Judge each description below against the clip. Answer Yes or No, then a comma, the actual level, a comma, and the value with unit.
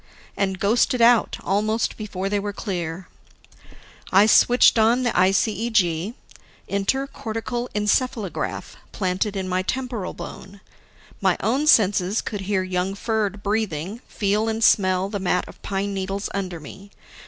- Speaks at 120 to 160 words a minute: Yes, slow, 135 wpm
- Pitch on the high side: Yes, high, 200 Hz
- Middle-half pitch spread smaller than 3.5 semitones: Yes, average, 2.9 semitones